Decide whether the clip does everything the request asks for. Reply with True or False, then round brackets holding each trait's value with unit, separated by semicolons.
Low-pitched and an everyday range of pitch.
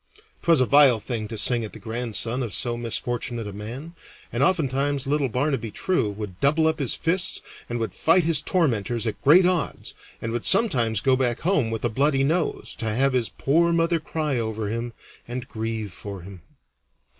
True (125 Hz; 5.0 semitones)